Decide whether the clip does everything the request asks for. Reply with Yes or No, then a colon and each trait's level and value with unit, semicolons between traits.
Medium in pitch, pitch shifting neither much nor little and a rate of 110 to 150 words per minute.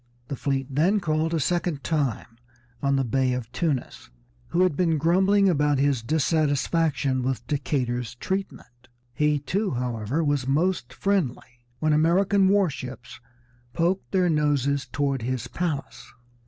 Yes: medium, 145 Hz; average, 4.5 semitones; average, 140 wpm